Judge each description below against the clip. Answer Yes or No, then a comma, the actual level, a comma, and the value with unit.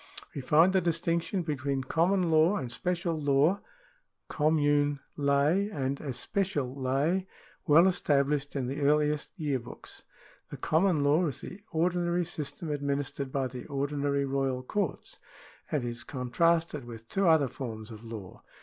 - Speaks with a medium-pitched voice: Yes, medium, 145 Hz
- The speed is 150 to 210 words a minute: No, average, 140 wpm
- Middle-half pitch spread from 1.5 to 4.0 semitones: Yes, average, 3.7 semitones